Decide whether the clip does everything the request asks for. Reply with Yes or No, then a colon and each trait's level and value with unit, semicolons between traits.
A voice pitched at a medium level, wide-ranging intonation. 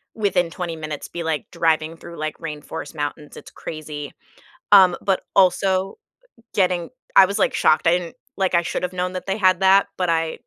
No: medium, 175 Hz; average, 2.9 semitones